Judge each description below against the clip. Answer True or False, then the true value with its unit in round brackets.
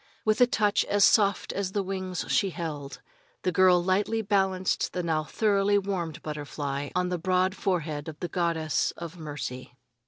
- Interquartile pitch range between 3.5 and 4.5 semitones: True (3.8 semitones)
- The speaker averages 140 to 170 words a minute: True (165 wpm)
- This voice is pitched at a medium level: True (180 Hz)